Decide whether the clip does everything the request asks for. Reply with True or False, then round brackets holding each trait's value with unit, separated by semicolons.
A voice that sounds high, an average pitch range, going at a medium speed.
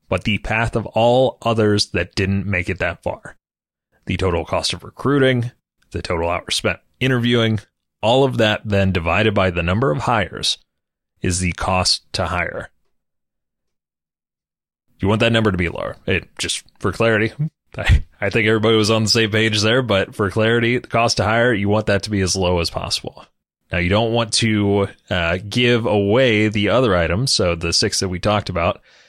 False (105 Hz; 3.6 semitones; 190 wpm)